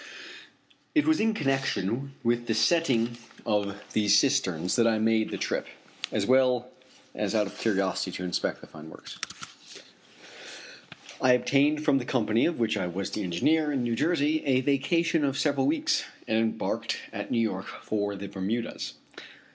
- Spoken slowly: No, average, 165 wpm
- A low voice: Yes, low, 120 Hz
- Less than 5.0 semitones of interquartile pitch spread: No, average, 5.3 semitones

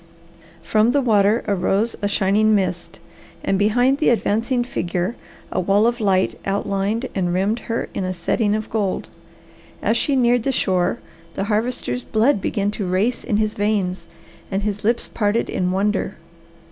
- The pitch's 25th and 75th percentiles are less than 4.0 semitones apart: Yes, average, 2.9 semitones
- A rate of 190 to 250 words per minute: No, average, 160 wpm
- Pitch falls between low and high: No, high, 210 Hz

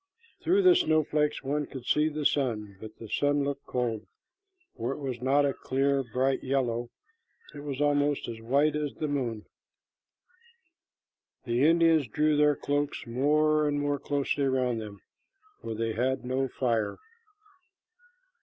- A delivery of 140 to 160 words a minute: Yes, average, 145 wpm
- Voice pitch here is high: No, medium, 140 Hz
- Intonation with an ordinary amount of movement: Yes, average, 3.3 semitones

